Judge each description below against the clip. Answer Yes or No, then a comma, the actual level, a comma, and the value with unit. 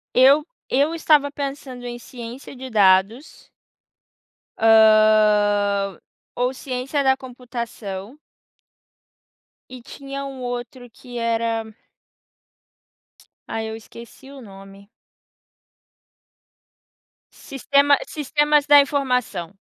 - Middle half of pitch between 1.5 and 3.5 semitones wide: No, average, 3.9 semitones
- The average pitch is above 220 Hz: Yes, high, 245 Hz